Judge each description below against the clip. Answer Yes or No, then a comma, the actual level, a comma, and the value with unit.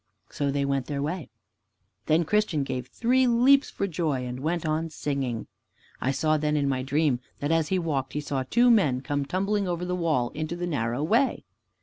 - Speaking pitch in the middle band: Yes, medium, 155 Hz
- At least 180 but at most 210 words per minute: Yes, average, 200 wpm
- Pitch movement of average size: Yes, average, 4.5 semitones